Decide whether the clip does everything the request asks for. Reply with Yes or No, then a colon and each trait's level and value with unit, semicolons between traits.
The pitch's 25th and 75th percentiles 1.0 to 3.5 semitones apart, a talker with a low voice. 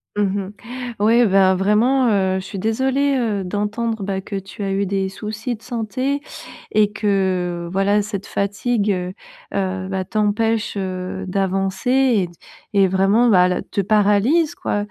No: average, 2.7 semitones; high, 200 Hz